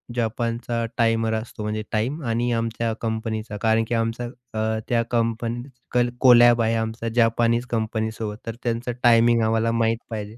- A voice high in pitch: No, low, 115 Hz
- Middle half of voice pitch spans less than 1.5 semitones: Yes, narrow, 1.1 semitones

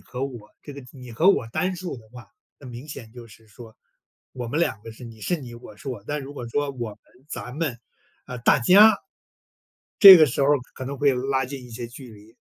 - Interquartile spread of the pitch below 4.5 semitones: Yes, average, 3.5 semitones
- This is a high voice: No, low, 125 Hz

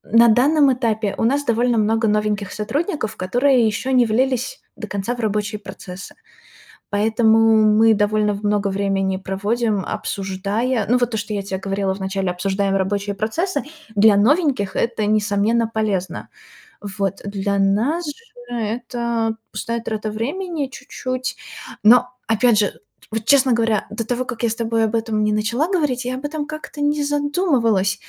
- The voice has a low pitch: No, high, 220 Hz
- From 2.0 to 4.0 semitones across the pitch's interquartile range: Yes, average, 3.4 semitones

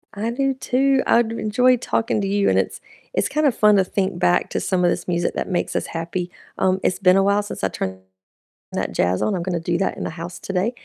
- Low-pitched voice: No, high, 195 Hz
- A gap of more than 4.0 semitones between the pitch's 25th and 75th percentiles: Yes, average, 4.5 semitones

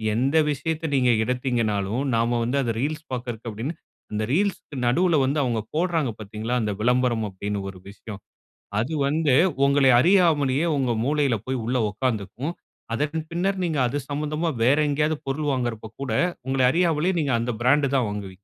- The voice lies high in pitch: No, low, 130 Hz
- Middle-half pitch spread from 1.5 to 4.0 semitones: No, average, 4.6 semitones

